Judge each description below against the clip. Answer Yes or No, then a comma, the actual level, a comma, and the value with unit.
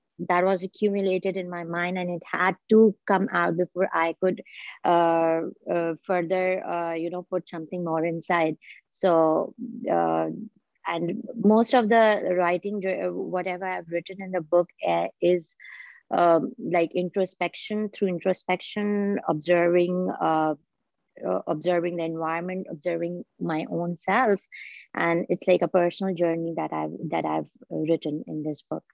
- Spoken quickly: No, average, 145 wpm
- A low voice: No, medium, 175 Hz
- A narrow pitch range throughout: Yes, narrow, 2.2 semitones